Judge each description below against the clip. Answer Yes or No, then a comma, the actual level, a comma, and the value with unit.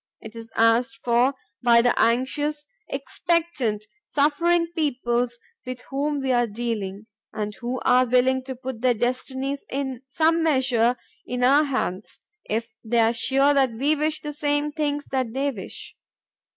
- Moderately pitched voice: No, very high, 255 Hz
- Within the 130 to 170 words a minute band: Yes, average, 150 wpm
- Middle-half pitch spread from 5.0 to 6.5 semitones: No, average, 3.5 semitones